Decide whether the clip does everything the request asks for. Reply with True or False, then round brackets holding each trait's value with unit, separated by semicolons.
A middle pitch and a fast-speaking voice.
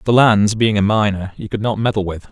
False (105 Hz; 260 wpm)